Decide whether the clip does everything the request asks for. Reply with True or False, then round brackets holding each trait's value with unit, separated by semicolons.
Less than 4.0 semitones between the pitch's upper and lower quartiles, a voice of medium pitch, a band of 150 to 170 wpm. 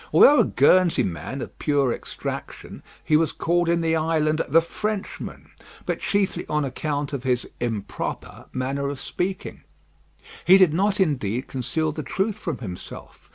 False (4.6 semitones; 155 Hz; 155 wpm)